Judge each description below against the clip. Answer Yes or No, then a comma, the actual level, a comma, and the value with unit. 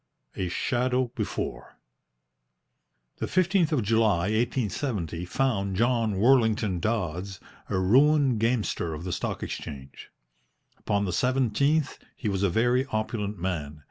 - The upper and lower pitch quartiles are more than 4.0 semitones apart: Yes, wide, 5.4 semitones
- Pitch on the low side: Yes, low, 110 Hz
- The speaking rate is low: Yes, slow, 120 wpm